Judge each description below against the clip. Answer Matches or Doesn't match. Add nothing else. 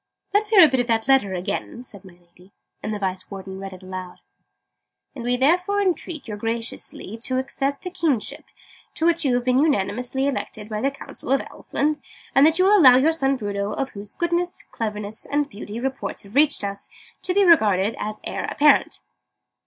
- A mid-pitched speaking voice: Doesn't match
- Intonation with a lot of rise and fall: Matches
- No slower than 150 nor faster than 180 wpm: Doesn't match